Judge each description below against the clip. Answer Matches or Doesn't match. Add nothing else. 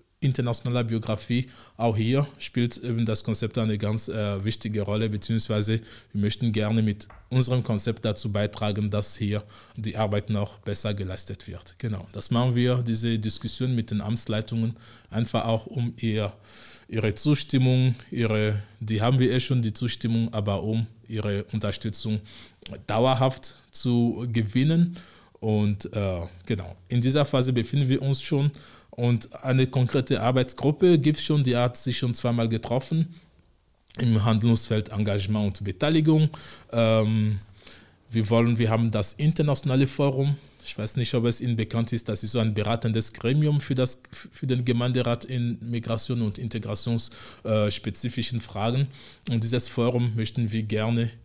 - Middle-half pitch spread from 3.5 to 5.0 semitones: Doesn't match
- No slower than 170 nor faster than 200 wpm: Doesn't match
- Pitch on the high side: Doesn't match